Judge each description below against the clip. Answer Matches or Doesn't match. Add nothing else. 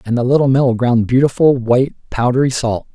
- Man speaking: Matches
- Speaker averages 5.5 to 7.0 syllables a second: Matches